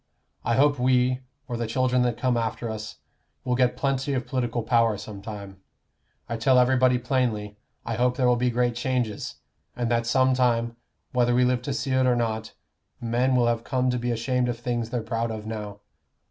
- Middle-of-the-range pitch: No, low, 120 Hz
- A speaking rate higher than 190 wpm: Yes, average, 200 wpm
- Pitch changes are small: Yes, narrow, 1.7 semitones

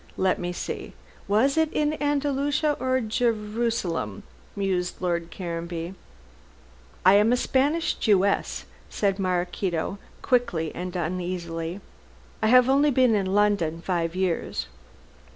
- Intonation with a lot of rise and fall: Yes, wide, 6.1 semitones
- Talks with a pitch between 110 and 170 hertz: No, high, 195 Hz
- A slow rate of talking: Yes, slow, 115 wpm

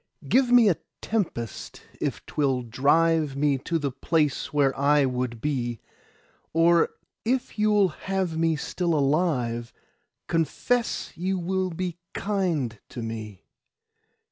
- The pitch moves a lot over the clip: Yes, wide, 5.7 semitones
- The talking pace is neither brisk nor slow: No, slow, 120 wpm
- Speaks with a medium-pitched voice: Yes, medium, 155 Hz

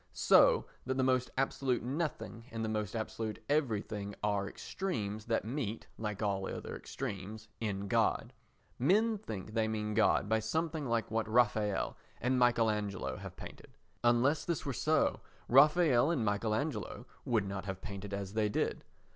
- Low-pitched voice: Yes, low, 115 Hz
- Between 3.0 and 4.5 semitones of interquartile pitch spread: Yes, average, 3.8 semitones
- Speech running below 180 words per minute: Yes, average, 160 wpm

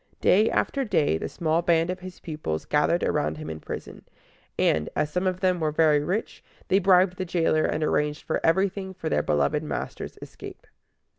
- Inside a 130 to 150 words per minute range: No, average, 180 wpm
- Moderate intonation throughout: Yes, average, 3.8 semitones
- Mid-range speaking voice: Yes, medium, 165 Hz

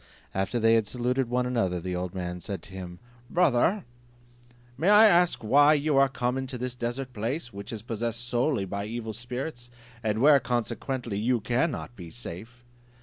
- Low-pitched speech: Yes, low, 120 Hz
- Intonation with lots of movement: No, average, 3.7 semitones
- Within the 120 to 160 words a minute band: No, average, 175 wpm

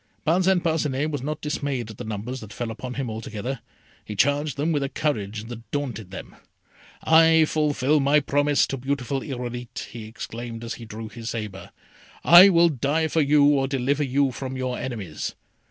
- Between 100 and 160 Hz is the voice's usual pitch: Yes, low, 135 Hz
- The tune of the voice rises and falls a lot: No, average, 4.2 semitones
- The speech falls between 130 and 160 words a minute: No, average, 175 wpm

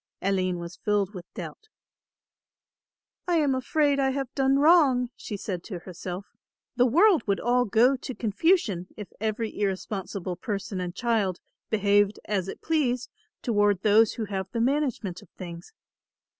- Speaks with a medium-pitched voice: No, high, 215 Hz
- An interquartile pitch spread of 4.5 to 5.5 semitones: Yes, average, 5.2 semitones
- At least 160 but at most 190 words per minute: No, average, 150 wpm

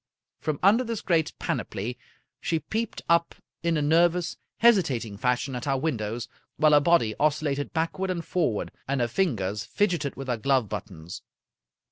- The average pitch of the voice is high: No, medium, 145 Hz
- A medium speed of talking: Yes, average, 160 wpm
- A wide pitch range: Yes, wide, 5.8 semitones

